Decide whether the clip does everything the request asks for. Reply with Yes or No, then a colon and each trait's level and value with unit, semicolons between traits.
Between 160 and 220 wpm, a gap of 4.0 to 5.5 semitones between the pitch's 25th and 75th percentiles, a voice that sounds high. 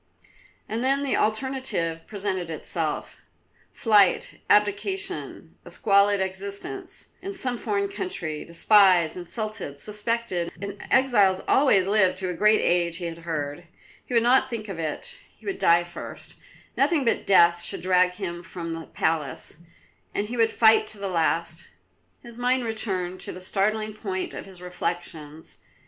No: average, 150 wpm; average, 4.7 semitones; high, 195 Hz